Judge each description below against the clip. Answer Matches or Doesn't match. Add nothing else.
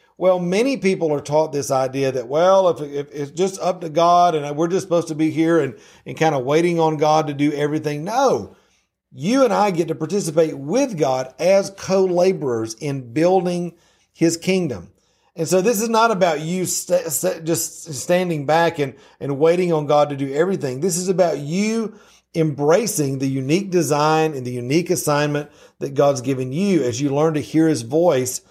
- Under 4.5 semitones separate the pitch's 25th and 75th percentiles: Matches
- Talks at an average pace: Matches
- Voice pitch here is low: Doesn't match